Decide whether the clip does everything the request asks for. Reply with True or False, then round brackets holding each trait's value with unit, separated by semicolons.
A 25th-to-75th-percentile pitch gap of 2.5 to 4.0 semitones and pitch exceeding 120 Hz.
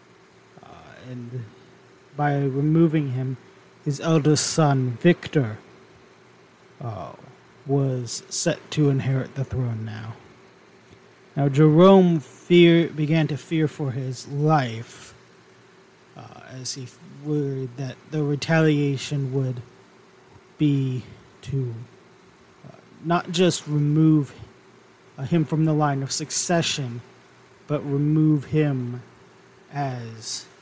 True (3.4 semitones; 140 Hz)